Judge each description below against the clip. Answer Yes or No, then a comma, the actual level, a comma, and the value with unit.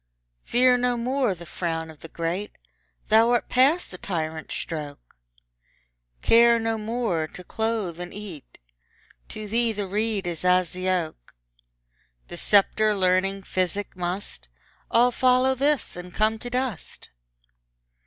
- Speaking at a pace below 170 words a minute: Yes, slow, 135 wpm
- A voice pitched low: No, high, 205 Hz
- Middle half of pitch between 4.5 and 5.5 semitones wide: Yes, average, 4.9 semitones